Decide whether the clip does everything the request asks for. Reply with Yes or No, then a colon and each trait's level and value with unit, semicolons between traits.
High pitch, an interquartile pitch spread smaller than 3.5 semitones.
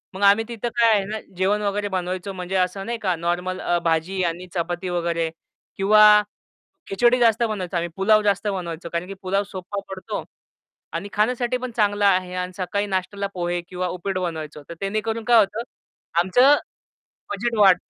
Yes: high, 195 Hz; average, 2.8 semitones